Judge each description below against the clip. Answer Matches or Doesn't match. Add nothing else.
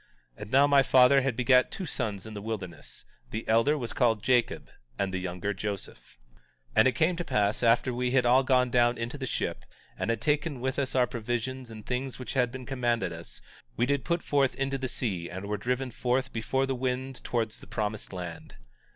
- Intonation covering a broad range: Doesn't match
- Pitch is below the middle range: Matches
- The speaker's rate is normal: Doesn't match